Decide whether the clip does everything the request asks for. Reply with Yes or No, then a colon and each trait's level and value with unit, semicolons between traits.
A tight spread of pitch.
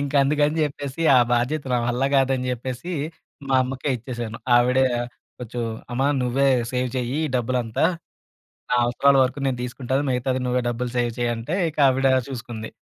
Yes: narrow, 1.9 semitones